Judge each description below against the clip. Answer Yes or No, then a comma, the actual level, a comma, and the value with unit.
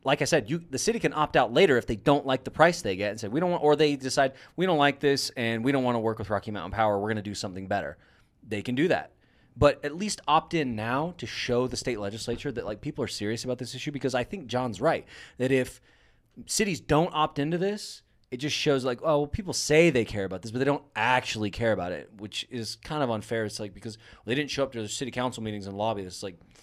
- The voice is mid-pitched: No, low, 125 Hz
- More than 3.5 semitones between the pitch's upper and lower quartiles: Yes, average, 4.9 semitones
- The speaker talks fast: Yes, fast, 270 wpm